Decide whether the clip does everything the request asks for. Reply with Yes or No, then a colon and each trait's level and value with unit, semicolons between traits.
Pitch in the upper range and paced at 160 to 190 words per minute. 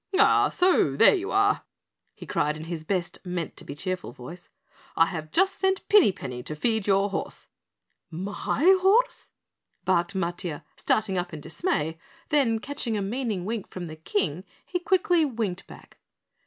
Yes: high, 195 Hz; average, 165 wpm